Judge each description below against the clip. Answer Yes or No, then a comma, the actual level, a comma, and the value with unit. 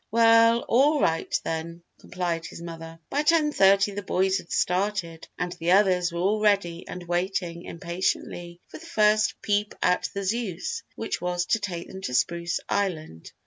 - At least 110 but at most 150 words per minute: No, average, 170 wpm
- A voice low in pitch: No, medium, 185 Hz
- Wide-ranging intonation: No, average, 3.4 semitones